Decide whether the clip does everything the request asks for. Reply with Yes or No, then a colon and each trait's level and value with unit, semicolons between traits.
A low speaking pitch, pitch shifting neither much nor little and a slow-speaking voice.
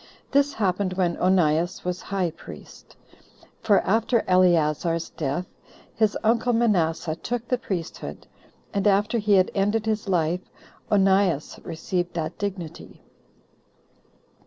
No: high, 190 Hz; average, 3.7 semitones; slow, 115 wpm